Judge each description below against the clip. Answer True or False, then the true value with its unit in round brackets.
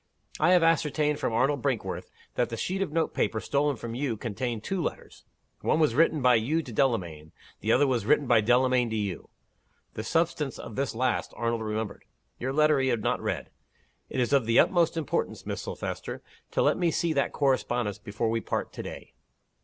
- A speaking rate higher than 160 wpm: True (200 wpm)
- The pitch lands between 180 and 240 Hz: False (125 Hz)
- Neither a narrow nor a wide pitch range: True (4.8 semitones)